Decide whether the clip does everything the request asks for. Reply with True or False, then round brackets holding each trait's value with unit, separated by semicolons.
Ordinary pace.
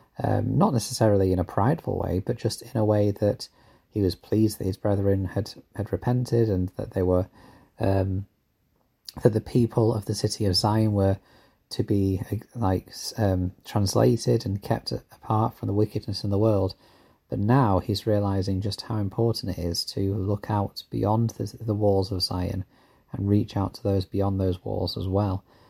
True (180 wpm)